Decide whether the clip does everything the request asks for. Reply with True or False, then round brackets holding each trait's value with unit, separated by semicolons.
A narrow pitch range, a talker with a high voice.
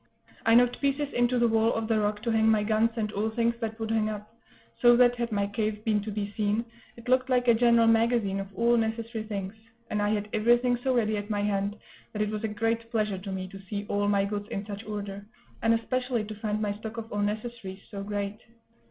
True (2.0 semitones; 220 Hz)